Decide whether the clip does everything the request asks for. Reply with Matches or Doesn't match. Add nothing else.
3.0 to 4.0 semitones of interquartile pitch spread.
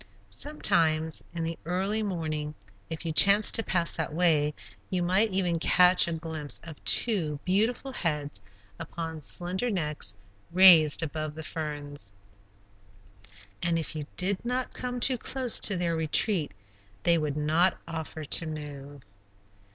Matches